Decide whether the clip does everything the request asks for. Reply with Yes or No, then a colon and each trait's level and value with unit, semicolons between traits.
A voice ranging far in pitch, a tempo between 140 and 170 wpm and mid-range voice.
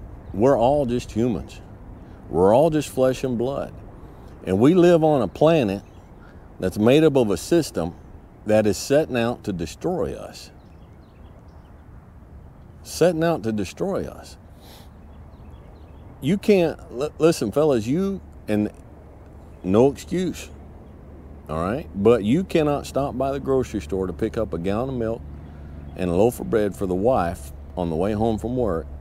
No: wide, 7.3 semitones; average, 155 wpm; very low, 95 Hz